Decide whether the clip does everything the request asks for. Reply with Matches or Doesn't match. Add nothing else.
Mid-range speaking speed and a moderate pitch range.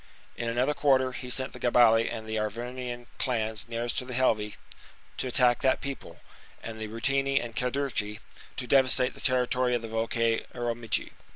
Doesn't match